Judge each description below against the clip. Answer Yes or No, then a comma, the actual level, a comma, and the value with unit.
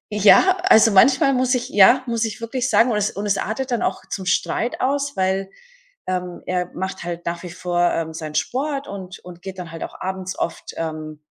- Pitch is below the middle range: No, high, 195 Hz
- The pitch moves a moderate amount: No, wide, 5.8 semitones